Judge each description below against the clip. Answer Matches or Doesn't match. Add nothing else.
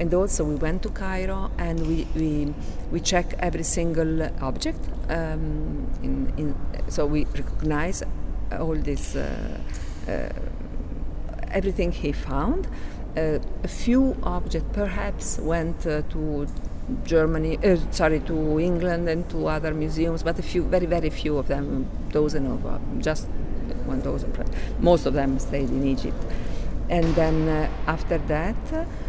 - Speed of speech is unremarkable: Matches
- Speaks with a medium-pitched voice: Matches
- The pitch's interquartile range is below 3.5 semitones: Matches